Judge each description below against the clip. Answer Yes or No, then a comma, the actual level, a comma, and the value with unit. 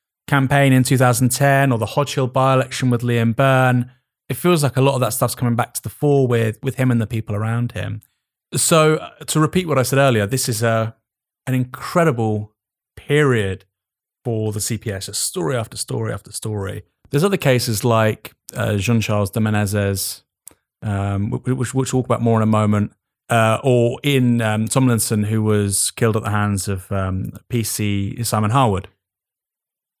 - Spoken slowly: No, average, 175 wpm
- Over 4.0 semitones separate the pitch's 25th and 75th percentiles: No, average, 3.7 semitones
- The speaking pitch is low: Yes, low, 120 Hz